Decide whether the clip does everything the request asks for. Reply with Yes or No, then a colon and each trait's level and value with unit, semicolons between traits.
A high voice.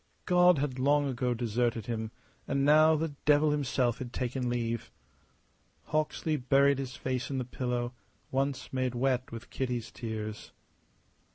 No: low, 130 Hz